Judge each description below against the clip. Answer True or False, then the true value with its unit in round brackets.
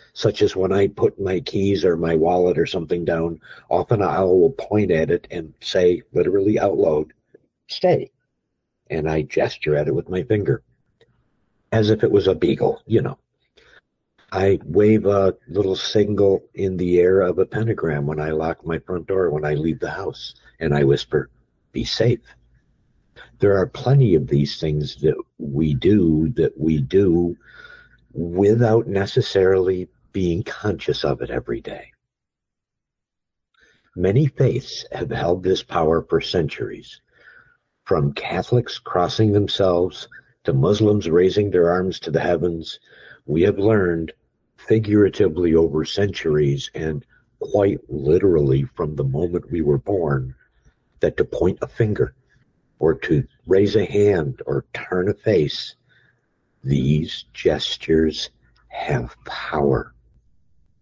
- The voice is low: True (90 Hz)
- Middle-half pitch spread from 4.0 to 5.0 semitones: True (4.4 semitones)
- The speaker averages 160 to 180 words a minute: False (140 wpm)